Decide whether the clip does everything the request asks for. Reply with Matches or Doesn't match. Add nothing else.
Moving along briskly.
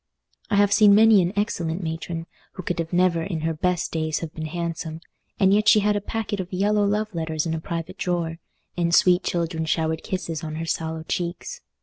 Matches